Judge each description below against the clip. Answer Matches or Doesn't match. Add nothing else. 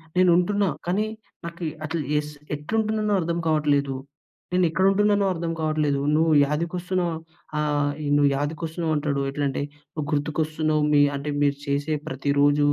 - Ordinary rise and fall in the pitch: Matches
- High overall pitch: Doesn't match